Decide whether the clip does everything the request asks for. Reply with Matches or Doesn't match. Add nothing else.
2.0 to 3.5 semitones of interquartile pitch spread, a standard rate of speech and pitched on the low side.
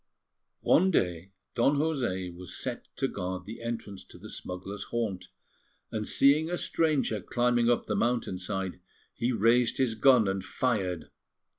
Doesn't match